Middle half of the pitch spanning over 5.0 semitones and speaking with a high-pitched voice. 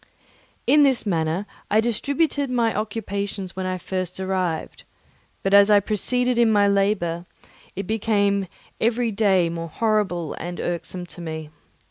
No: average, 3.8 semitones; high, 200 Hz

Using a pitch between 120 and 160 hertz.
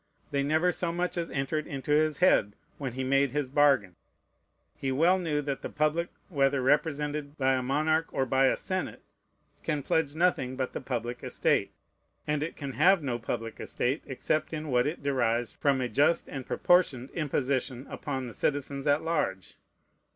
Yes: medium, 140 Hz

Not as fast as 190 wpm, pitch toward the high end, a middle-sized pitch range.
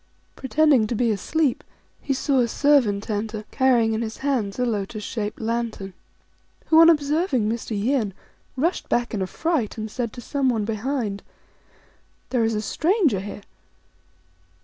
Yes: average, 160 wpm; high, 235 Hz; average, 4.5 semitones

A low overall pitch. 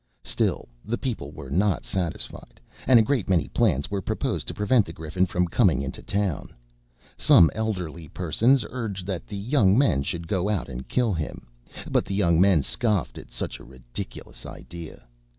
Yes: very low, 95 Hz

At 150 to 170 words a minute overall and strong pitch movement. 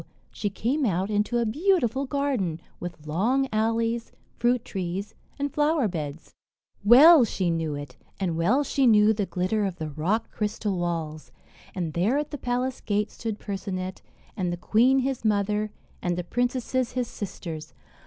Yes: average, 160 wpm; wide, 5.8 semitones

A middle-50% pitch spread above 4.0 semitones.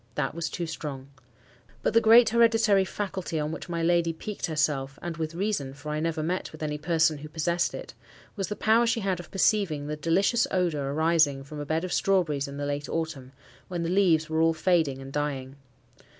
No: average, 3.7 semitones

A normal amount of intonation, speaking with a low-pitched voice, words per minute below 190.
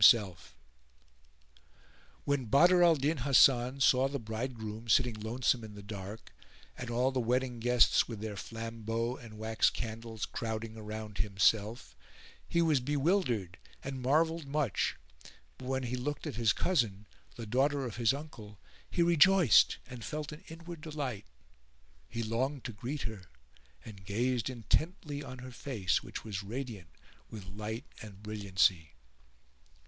Yes: average, 4.2 semitones; low, 120 Hz; average, 145 wpm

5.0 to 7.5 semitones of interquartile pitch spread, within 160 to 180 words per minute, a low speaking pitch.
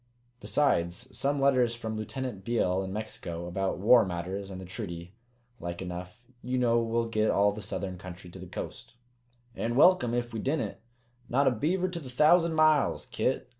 Yes: wide, 5.5 semitones; average, 175 wpm; low, 115 Hz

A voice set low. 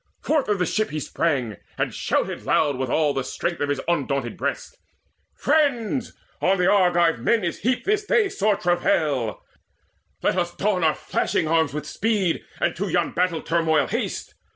No: medium, 175 Hz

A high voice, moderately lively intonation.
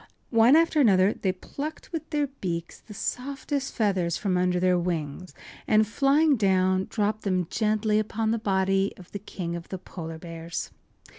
Yes: high, 200 Hz; average, 4.0 semitones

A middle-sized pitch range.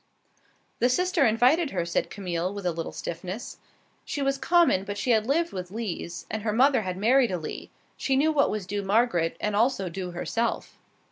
No: wide, 6.3 semitones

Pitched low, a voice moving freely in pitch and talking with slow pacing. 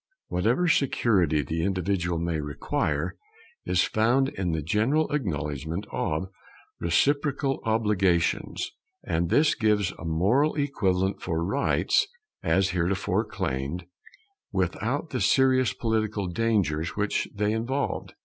Yes: low, 100 Hz; wide, 6.5 semitones; slow, 110 wpm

